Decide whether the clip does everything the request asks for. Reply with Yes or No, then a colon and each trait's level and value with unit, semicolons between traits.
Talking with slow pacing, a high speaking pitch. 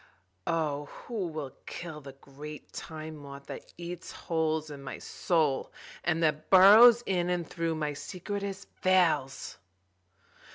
No: slow, 130 wpm; medium, 160 Hz